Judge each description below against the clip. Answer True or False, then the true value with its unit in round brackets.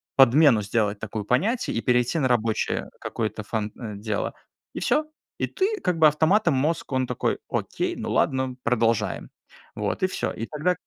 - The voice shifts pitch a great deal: True (6.2 semitones)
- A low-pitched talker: True (125 Hz)